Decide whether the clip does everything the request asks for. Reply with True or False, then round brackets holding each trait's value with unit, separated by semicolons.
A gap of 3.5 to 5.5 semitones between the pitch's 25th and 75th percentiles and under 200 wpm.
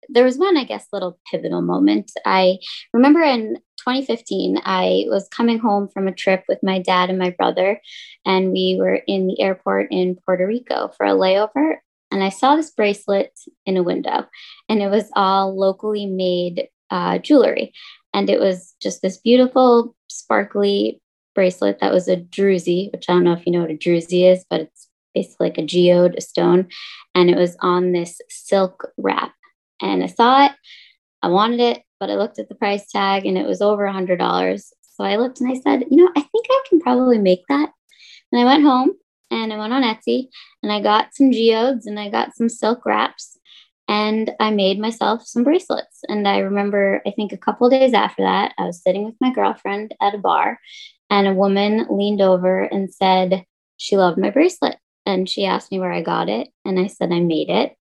False (5.0 semitones; 205 wpm)